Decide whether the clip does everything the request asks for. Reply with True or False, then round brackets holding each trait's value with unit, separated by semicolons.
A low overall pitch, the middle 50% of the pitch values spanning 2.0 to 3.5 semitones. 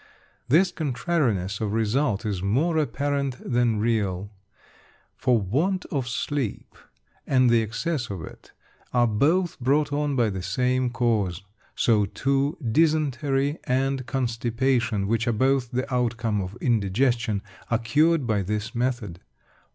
False (120 Hz; 4.2 semitones)